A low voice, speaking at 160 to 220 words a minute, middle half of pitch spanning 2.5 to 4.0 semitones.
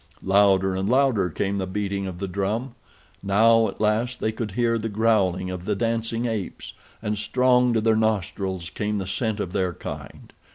Yes: low, 105 Hz; average, 180 wpm; average, 2.9 semitones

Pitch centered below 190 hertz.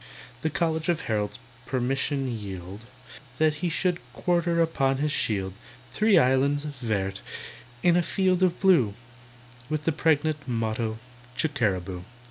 Yes: medium, 140 Hz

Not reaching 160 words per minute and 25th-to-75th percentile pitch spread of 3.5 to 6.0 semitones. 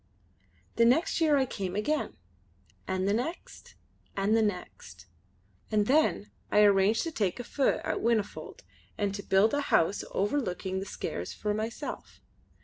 Yes: average, 150 wpm; average, 3.9 semitones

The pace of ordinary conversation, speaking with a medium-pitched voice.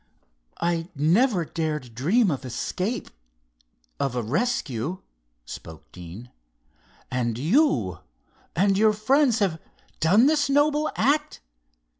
No: slow, 105 wpm; medium, 180 Hz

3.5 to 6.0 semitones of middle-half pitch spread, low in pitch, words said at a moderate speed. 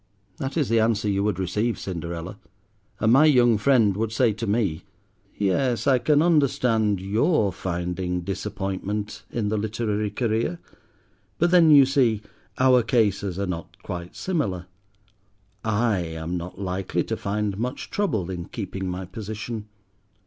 Yes: average, 4.1 semitones; low, 105 Hz; average, 145 wpm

